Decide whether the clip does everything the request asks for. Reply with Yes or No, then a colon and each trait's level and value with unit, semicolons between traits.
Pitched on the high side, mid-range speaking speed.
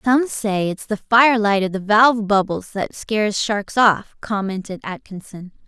Yes: high, 210 Hz; average, 170 wpm